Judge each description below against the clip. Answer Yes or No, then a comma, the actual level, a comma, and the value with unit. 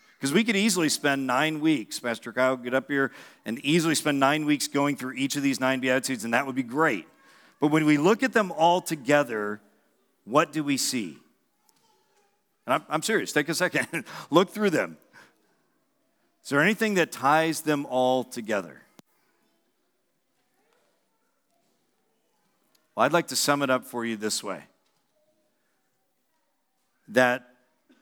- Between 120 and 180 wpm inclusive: Yes, average, 150 wpm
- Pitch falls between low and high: Yes, medium, 145 Hz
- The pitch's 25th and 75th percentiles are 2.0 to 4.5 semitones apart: No, average, 5.1 semitones